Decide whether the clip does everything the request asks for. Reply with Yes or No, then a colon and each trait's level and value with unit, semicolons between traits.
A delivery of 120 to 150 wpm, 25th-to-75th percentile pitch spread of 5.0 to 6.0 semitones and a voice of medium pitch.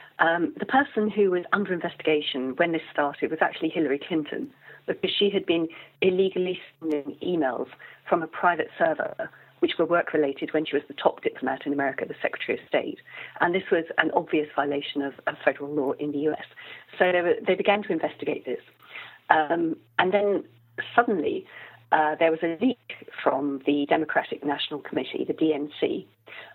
No: average, 175 wpm; wide, 5.5 semitones; medium, 165 Hz